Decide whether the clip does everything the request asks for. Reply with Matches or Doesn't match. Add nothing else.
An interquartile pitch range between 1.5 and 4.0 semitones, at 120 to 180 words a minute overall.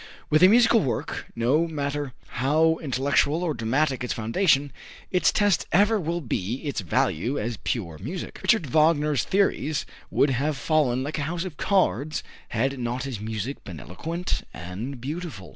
Doesn't match